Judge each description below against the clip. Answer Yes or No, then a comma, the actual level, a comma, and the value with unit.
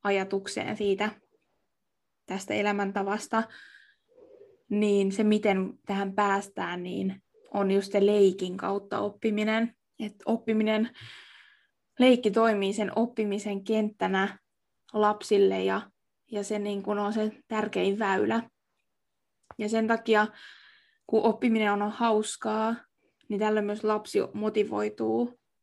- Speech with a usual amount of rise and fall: No, narrow, 1.9 semitones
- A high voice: Yes, high, 210 Hz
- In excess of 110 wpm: No, average, 105 wpm